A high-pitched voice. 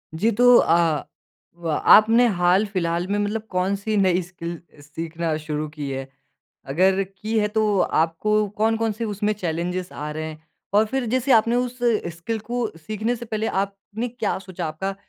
Yes: high, 195 Hz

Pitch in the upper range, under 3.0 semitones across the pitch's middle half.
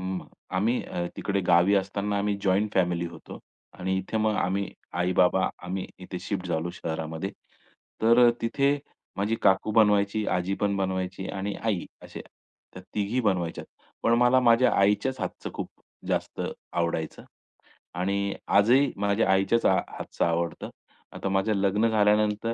No: low, 100 Hz; narrow, 2.6 semitones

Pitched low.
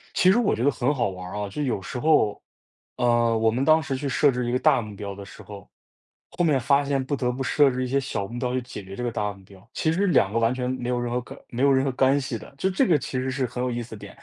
Yes: low, 125 Hz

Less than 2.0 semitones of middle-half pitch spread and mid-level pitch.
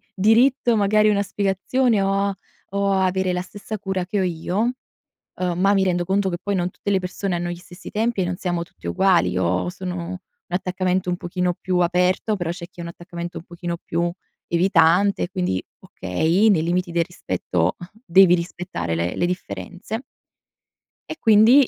No: narrow, 2.4 semitones; medium, 180 Hz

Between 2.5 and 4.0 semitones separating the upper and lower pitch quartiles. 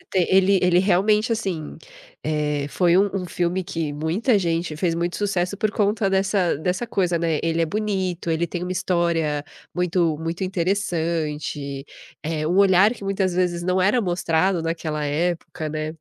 Yes: average, 2.9 semitones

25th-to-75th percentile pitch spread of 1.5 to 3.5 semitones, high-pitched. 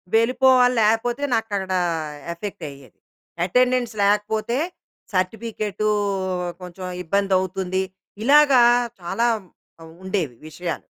No: average, 4.1 semitones; high, 205 Hz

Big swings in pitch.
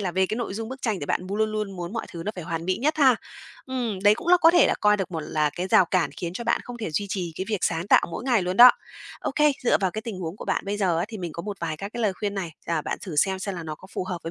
No: average, 4.1 semitones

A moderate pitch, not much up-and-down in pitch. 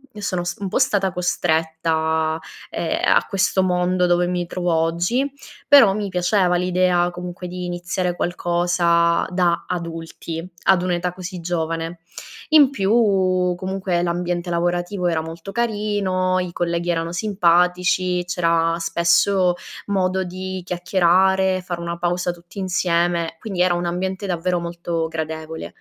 Yes: medium, 180 Hz; narrow, 1.5 semitones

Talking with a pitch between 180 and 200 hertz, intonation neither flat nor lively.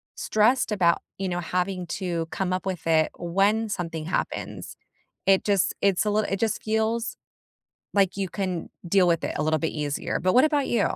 Yes: high, 190 Hz; average, 3.5 semitones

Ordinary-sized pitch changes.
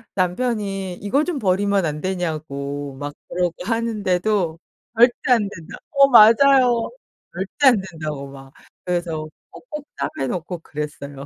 No: wide, 6.8 semitones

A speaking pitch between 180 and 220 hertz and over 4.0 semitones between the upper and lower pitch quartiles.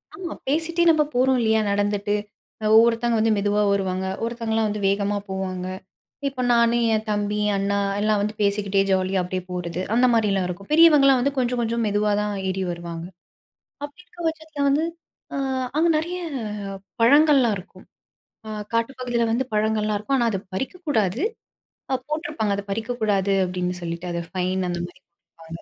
Yes: high, 215 Hz; average, 4.5 semitones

